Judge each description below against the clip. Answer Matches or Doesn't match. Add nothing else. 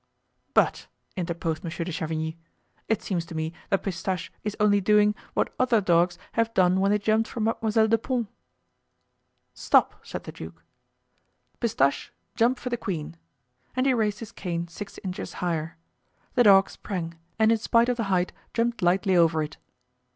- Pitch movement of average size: Matches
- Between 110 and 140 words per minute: Doesn't match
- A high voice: Matches